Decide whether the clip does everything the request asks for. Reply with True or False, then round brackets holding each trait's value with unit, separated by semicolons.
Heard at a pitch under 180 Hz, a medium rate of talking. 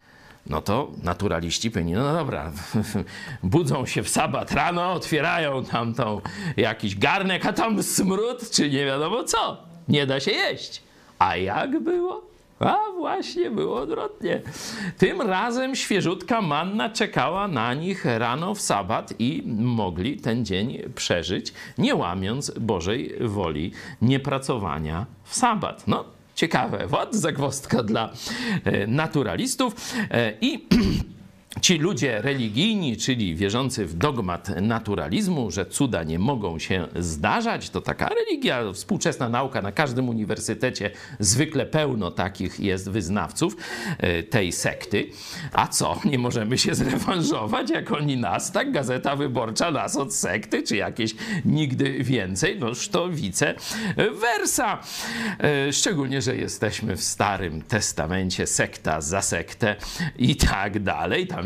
True (135 Hz; 125 wpm)